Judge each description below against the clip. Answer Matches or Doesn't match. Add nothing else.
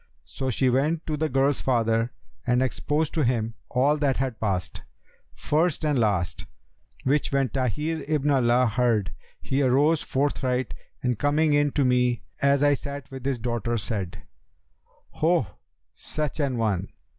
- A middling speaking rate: Matches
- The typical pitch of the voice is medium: Doesn't match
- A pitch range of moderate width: Matches